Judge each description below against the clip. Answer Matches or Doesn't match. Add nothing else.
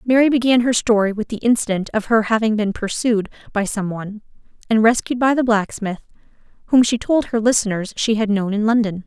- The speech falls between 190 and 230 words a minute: Matches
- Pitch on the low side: Doesn't match